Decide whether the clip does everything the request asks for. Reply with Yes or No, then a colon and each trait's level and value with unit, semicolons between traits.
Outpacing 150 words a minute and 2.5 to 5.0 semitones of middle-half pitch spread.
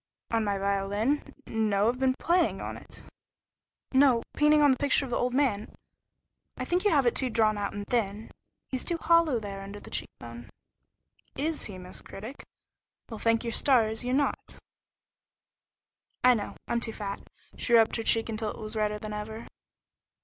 Yes: average, 180 wpm; average, 4.0 semitones